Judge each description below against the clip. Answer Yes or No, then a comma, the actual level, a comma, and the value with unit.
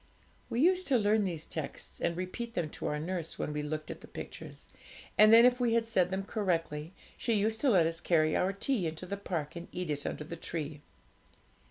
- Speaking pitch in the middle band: Yes, medium, 180 Hz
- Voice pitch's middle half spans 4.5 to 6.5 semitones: Yes, wide, 5.6 semitones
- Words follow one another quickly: Yes, fast, 220 wpm